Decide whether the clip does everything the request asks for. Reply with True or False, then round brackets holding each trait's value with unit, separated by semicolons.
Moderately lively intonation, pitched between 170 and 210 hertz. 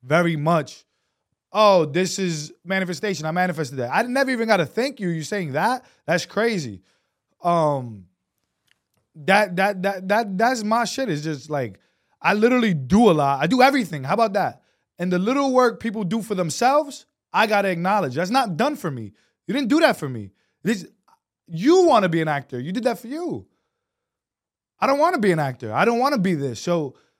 False (6.8 semitones; 190 Hz)